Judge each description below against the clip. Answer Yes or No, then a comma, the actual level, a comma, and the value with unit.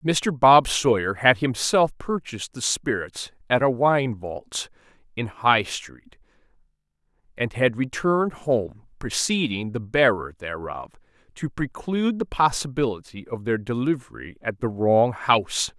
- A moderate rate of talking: No, slow, 130 wpm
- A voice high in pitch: No, low, 125 Hz